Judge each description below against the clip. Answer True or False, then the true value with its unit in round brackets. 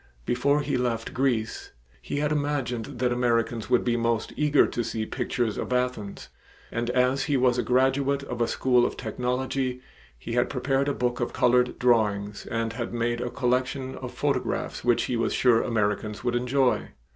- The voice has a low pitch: True (125 Hz)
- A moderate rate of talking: True (180 wpm)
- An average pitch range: False (2.0 semitones)